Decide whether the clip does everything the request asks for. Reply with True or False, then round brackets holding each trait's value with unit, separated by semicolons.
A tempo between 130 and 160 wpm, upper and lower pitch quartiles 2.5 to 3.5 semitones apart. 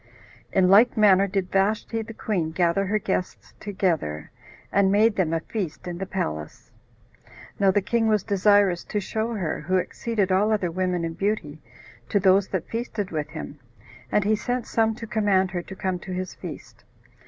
False (180 wpm; 2.8 semitones)